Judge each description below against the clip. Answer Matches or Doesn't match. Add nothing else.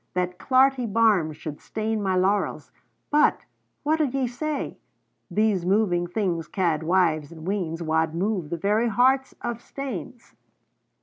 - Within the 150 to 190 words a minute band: Doesn't match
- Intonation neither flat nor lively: Doesn't match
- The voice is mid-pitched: Doesn't match